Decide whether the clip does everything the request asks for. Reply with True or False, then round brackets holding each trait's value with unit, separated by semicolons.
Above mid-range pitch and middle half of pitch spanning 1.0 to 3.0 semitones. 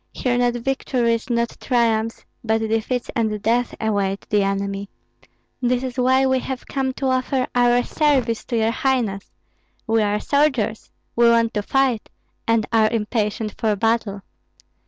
True (230 Hz; 2.6 semitones)